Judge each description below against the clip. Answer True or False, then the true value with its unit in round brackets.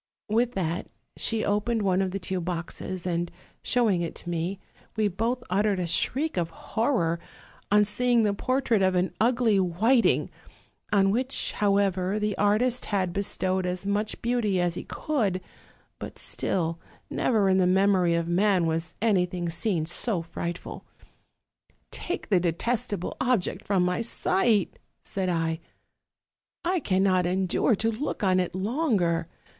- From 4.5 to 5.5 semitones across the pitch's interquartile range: False (3.7 semitones)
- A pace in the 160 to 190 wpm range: False (150 wpm)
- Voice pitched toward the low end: False (195 Hz)